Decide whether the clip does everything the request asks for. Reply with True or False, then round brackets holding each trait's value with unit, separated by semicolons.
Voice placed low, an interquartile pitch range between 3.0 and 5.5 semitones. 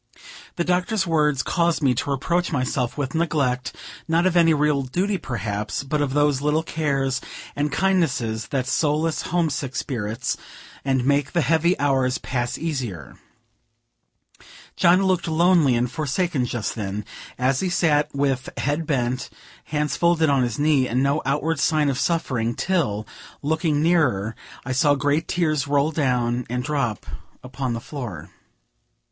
False (145 Hz; 4.2 semitones)